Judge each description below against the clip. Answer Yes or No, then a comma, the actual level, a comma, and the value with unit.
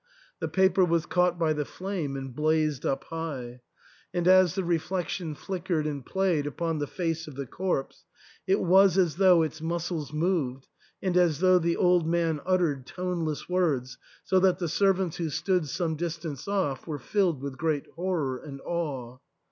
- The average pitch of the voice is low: No, medium, 165 Hz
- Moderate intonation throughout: Yes, average, 3.5 semitones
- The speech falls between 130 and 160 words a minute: No, average, 170 wpm